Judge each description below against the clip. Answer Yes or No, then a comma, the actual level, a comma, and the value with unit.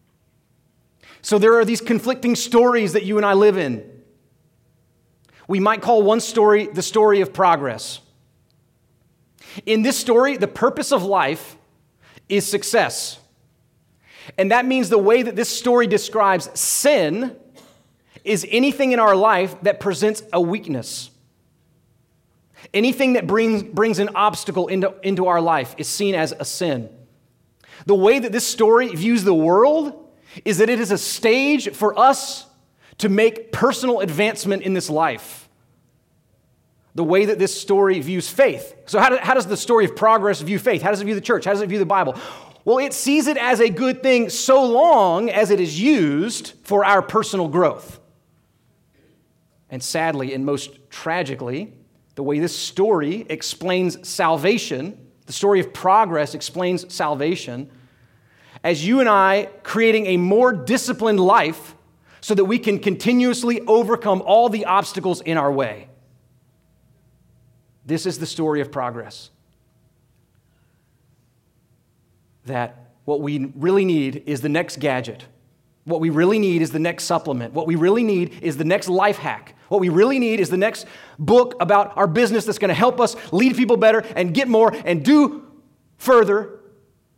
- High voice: Yes, high, 195 Hz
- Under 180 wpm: Yes, average, 160 wpm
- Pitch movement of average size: No, wide, 6.3 semitones